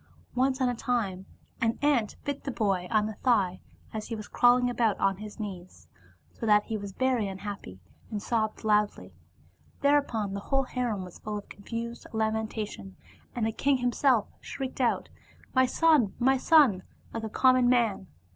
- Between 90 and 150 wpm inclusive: No, average, 185 wpm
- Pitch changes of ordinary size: Yes, average, 3.5 semitones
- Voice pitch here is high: Yes, high, 225 Hz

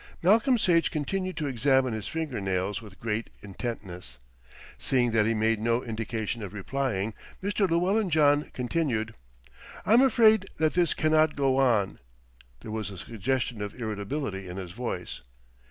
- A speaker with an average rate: Yes, average, 150 wpm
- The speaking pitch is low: Yes, low, 120 Hz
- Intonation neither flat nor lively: No, wide, 6.8 semitones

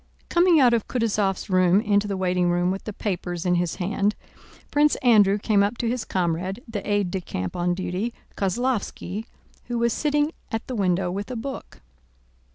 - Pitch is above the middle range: Yes, high, 200 Hz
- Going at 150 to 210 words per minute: Yes, average, 180 wpm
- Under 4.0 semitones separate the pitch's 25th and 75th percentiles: No, average, 4.3 semitones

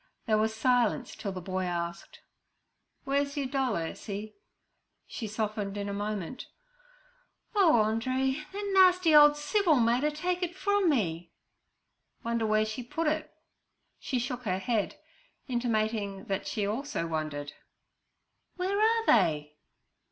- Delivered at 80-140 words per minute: Yes, slow, 135 wpm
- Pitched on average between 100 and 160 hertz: No, high, 235 Hz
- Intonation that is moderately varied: No, wide, 6.7 semitones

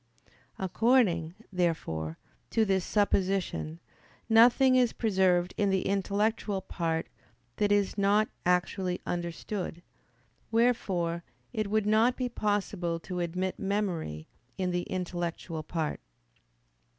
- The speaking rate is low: Yes, slow, 105 wpm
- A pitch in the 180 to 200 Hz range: Yes, high, 190 Hz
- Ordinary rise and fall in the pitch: Yes, average, 3.5 semitones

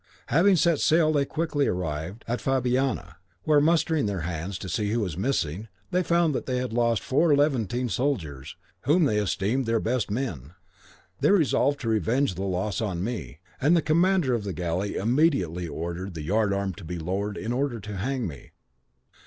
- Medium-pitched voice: No, low, 115 Hz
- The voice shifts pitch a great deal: Yes, wide, 7.2 semitones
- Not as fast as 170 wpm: No, average, 185 wpm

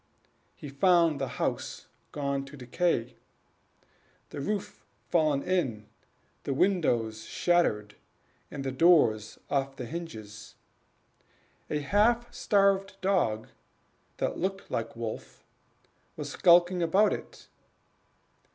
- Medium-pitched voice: Yes, medium, 150 Hz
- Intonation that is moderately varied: No, wide, 7.1 semitones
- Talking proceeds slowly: Yes, slow, 105 wpm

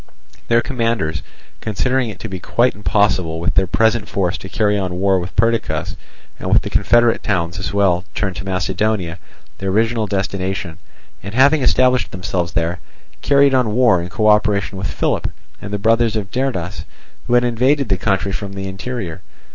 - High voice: No, low, 100 Hz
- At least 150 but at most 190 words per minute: Yes, average, 175 wpm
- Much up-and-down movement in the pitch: No, average, 3.8 semitones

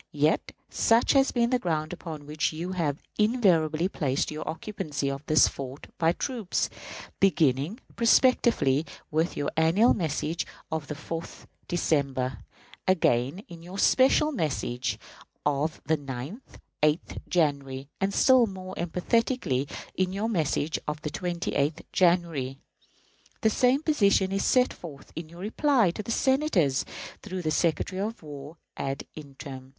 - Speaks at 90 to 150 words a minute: Yes, average, 140 wpm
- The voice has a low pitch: No, medium, 165 Hz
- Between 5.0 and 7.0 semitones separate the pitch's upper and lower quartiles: Yes, wide, 5.5 semitones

